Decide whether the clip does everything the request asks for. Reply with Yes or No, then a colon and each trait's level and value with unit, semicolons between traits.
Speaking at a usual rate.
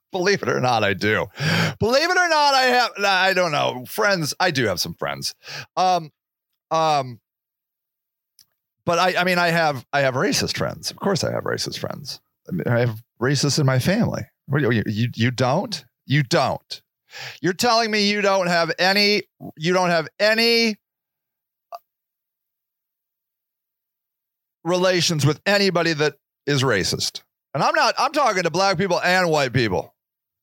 Yes: average, 160 wpm